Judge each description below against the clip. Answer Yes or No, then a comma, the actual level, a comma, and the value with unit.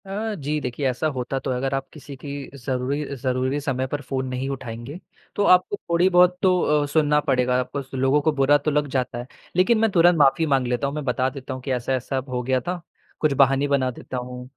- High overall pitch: No, low, 135 Hz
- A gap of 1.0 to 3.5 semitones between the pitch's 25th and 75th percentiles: Yes, average, 2.9 semitones